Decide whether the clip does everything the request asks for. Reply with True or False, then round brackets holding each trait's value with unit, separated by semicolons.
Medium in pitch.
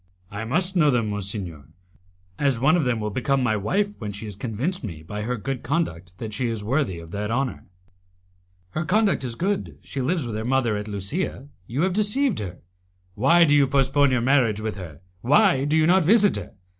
False (125 Hz)